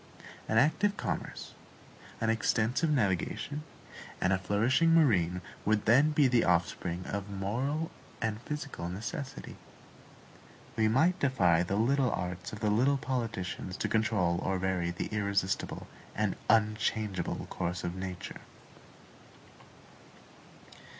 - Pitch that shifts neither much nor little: No, wide, 5.7 semitones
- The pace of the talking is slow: Yes, slow, 115 wpm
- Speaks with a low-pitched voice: Yes, low, 105 Hz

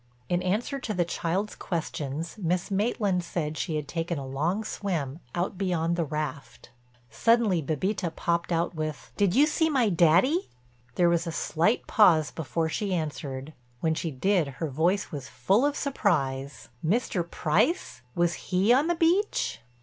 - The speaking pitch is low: No, medium, 170 Hz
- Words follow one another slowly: No, average, 160 wpm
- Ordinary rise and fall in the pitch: Yes, average, 4.7 semitones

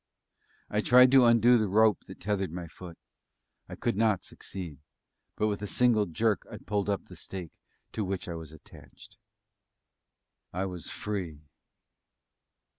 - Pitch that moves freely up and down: No, average, 3.4 semitones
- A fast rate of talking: No, average, 150 wpm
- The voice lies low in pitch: Yes, low, 100 Hz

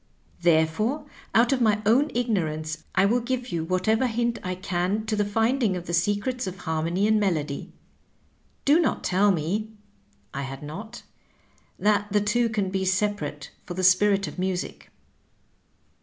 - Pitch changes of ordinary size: Yes, average, 4.0 semitones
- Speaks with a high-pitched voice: Yes, high, 200 Hz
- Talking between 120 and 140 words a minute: No, average, 165 wpm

